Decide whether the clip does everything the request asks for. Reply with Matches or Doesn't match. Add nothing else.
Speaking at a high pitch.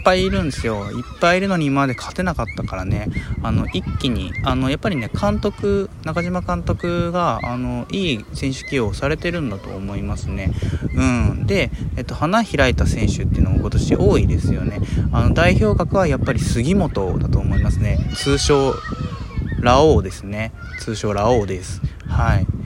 Doesn't match